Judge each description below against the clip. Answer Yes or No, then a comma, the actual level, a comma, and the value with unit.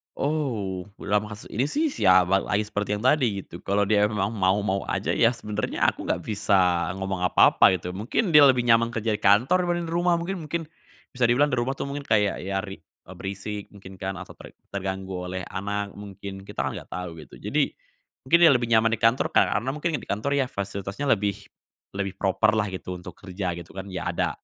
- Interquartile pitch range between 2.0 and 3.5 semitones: No, average, 4.1 semitones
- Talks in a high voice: No, low, 105 Hz